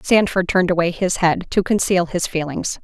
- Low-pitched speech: No, medium, 180 Hz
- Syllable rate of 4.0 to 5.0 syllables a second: No, 5.2 syllables/s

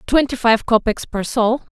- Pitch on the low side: No, high, 235 Hz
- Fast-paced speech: No, average, 170 wpm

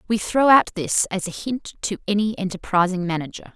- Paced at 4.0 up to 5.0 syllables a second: No, 5.3 syllables/s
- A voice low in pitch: No, high, 195 Hz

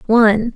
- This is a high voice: Yes, high, 220 Hz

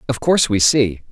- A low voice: Yes, low, 115 Hz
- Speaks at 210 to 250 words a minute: Yes, fast, 215 wpm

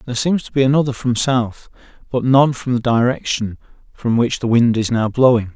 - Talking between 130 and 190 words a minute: No, fast, 205 wpm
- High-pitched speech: No, low, 120 Hz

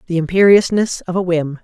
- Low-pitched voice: No, medium, 180 Hz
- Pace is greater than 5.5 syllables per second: Yes, 5.7 syllables/s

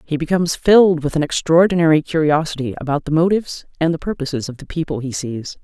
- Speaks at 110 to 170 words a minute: No, average, 180 wpm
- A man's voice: No, female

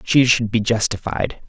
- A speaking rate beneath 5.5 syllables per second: Yes, 4.4 syllables/s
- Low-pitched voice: Yes, low, 110 Hz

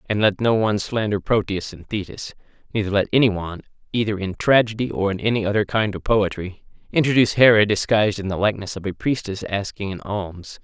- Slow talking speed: No, average, 190 wpm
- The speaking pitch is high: No, low, 105 Hz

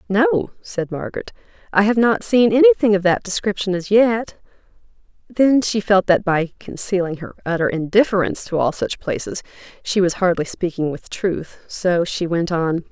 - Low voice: No, high, 195 Hz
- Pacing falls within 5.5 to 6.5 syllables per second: No, 4.8 syllables/s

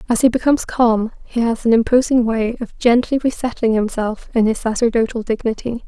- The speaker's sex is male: No, female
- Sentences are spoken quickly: No, average, 175 wpm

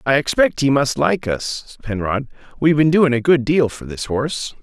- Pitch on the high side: No, low, 135 Hz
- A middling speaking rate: No, fast, 210 wpm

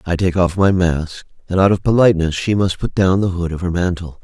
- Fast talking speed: Yes, fast, 255 wpm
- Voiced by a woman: No, male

